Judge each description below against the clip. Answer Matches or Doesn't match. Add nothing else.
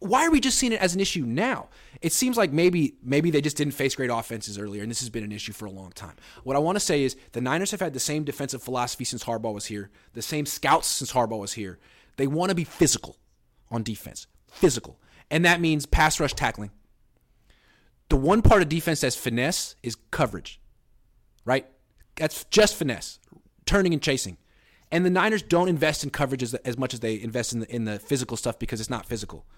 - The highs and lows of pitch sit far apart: Matches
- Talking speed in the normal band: Doesn't match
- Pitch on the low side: Matches